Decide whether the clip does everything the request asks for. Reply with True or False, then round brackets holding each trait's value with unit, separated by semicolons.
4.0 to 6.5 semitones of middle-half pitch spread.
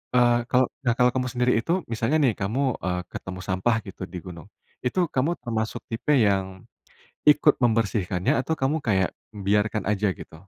True (4.4 semitones)